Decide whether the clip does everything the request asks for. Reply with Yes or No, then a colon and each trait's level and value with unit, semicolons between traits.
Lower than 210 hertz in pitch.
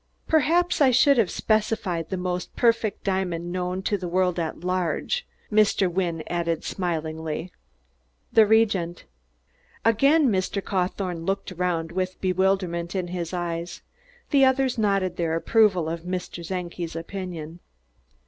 Yes: medium, 185 Hz